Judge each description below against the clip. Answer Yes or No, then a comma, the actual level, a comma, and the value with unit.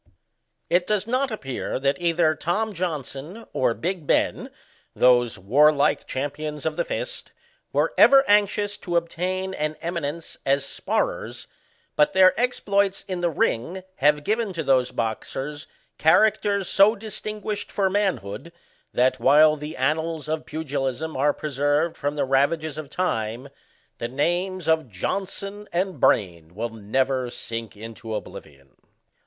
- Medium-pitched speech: Yes, medium, 155 Hz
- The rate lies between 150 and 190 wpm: No, slow, 135 wpm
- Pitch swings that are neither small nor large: No, wide, 6.1 semitones